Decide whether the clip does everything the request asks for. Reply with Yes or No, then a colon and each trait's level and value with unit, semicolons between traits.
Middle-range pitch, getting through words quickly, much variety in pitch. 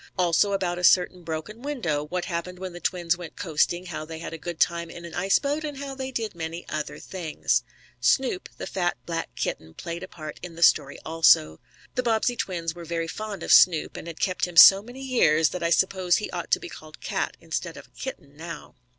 No: medium, 175 Hz; fast, 225 wpm; average, 3.1 semitones